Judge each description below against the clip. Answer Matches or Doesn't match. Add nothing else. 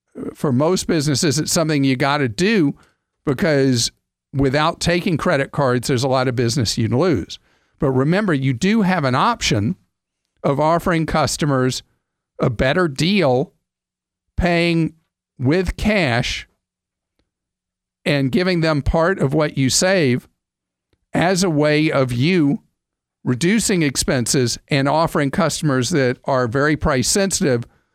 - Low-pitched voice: Doesn't match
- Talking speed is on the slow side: Matches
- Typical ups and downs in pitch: Matches